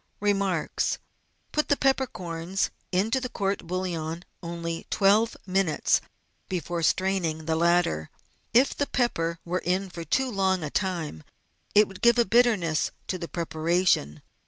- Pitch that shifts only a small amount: No, average, 3.4 semitones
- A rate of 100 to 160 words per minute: Yes, average, 140 wpm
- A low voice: No, medium, 185 Hz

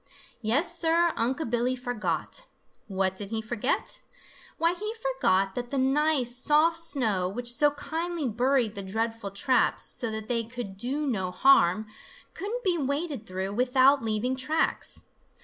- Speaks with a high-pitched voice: Yes, very high, 250 Hz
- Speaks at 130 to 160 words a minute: Yes, average, 150 wpm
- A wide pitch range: Yes, wide, 5.7 semitones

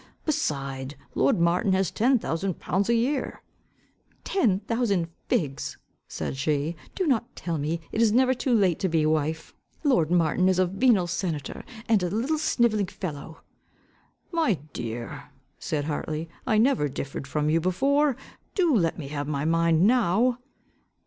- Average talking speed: Yes, average, 155 wpm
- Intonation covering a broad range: Yes, wide, 7.2 semitones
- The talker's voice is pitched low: No, medium, 180 Hz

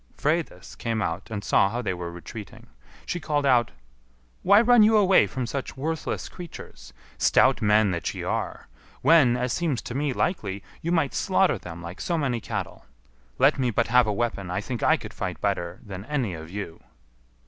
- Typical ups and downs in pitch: No, wide, 7.4 semitones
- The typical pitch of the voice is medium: No, low, 120 Hz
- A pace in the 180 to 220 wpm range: Yes, average, 190 wpm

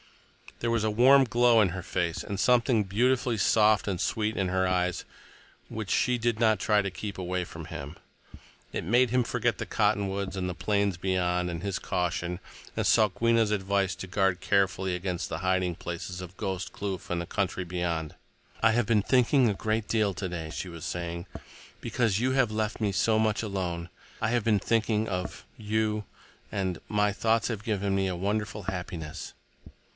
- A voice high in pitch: No, low, 100 Hz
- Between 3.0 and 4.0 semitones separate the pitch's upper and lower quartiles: Yes, average, 3.4 semitones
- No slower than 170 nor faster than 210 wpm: Yes, average, 180 wpm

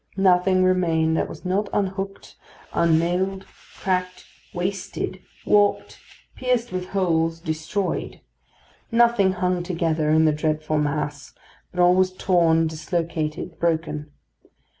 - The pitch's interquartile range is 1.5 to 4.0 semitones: Yes, average, 2.9 semitones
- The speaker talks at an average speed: No, slow, 110 wpm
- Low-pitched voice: No, medium, 180 Hz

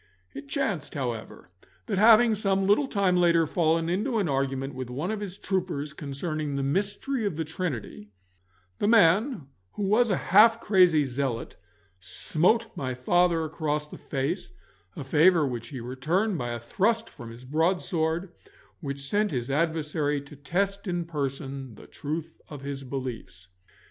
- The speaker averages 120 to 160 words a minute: Yes, average, 155 wpm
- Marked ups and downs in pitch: Yes, wide, 5.9 semitones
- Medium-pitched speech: Yes, medium, 160 Hz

